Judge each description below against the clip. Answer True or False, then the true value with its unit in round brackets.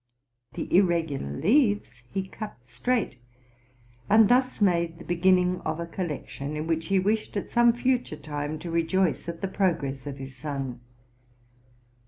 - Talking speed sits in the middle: True (160 wpm)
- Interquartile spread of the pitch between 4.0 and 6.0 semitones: True (5.2 semitones)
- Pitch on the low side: False (170 Hz)